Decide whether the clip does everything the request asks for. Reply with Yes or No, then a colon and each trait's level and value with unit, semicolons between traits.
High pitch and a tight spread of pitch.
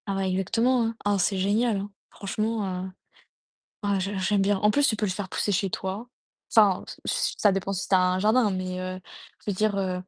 Yes: high, 200 Hz; narrow, 2.1 semitones